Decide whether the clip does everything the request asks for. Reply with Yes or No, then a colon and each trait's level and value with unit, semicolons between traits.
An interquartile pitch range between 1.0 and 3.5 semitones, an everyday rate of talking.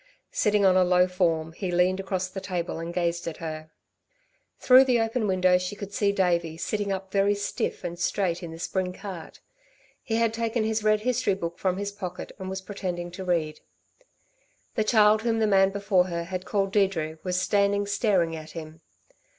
Yes: average, 2.8 semitones; average, 190 wpm